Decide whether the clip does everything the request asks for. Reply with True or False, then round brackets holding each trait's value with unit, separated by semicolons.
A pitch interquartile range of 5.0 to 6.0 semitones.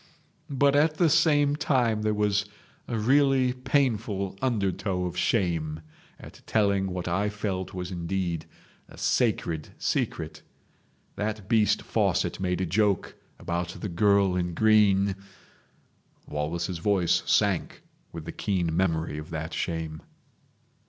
False (4.0 semitones)